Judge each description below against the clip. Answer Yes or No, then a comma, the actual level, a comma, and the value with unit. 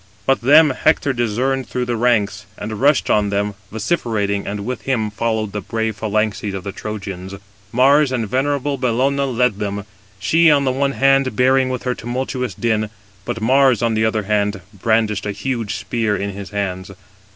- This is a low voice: Yes, low, 115 Hz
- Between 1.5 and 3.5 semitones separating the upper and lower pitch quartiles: No, average, 4.0 semitones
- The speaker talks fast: No, average, 175 wpm